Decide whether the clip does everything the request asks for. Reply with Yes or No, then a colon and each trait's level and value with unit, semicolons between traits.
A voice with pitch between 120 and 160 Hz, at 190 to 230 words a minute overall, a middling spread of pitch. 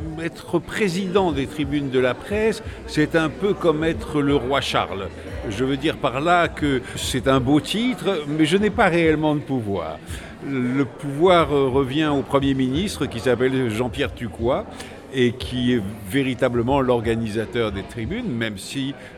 No: medium, 140 Hz; average, 160 wpm; average, 4.2 semitones